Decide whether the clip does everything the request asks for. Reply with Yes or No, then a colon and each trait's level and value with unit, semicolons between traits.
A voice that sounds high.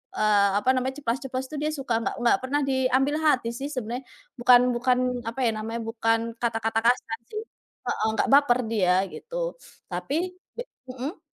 Yes: very high, 250 Hz